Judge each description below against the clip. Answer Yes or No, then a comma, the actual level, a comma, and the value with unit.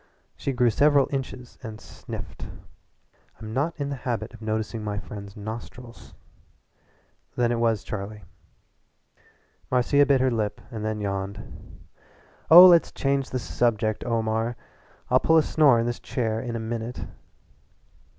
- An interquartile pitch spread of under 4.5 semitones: Yes, average, 3.1 semitones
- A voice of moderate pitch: No, low, 115 Hz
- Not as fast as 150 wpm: Yes, average, 140 wpm